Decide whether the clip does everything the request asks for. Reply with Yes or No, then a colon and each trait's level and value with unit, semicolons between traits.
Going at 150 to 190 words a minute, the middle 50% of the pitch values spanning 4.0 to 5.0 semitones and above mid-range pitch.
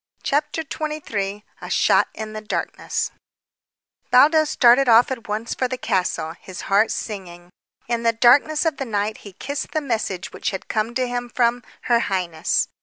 Yes: average, 170 wpm; average, 4.3 semitones; high, 230 Hz